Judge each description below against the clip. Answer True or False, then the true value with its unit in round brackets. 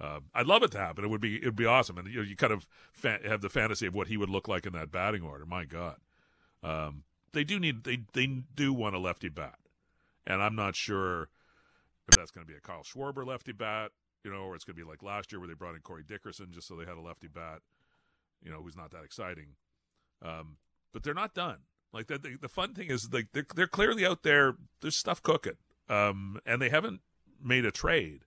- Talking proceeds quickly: True (250 wpm)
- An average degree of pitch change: False (7.3 semitones)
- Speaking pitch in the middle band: False (100 Hz)